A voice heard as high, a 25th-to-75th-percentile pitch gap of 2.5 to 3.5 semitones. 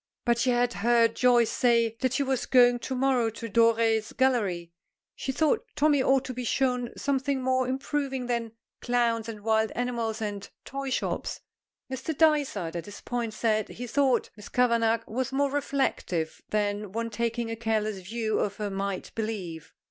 Yes: high, 235 Hz; average, 3.0 semitones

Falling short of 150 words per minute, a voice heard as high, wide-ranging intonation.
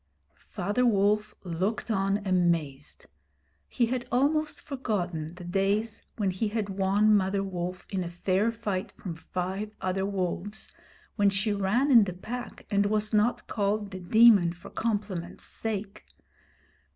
No: average, 140 wpm; high, 200 Hz; average, 2.7 semitones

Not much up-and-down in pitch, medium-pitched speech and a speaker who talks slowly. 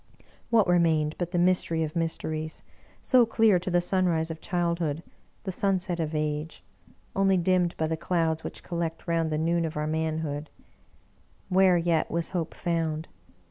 No: narrow, 1.9 semitones; medium, 170 Hz; average, 160 wpm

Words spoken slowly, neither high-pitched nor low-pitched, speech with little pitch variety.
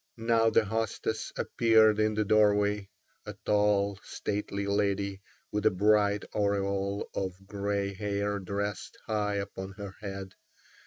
No: slow, 125 wpm; low, 100 Hz; narrow, 1.1 semitones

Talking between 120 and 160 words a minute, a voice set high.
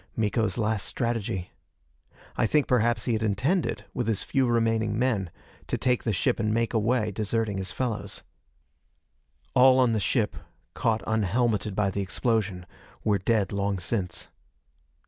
No: average, 145 wpm; low, 110 Hz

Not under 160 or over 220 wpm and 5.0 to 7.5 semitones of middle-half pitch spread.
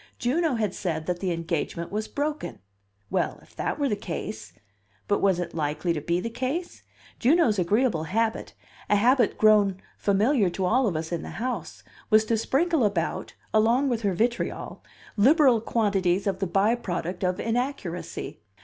Yes: average, 165 wpm; wide, 5.4 semitones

